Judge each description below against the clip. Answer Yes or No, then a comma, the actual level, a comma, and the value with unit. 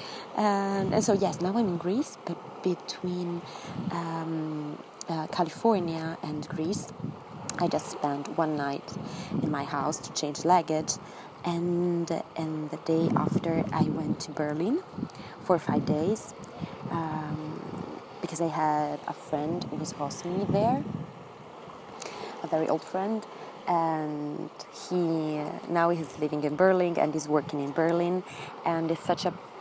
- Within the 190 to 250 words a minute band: No, average, 140 wpm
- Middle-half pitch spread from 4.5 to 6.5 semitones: No, average, 2.7 semitones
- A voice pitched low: No, medium, 165 Hz